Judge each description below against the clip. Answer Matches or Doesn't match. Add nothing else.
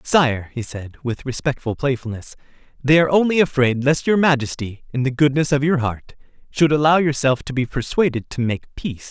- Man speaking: Matches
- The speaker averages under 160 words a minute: Doesn't match